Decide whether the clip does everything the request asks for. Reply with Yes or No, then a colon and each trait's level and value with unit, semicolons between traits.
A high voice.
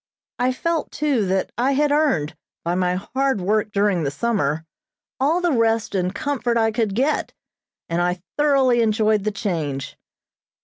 Yes: high, 220 Hz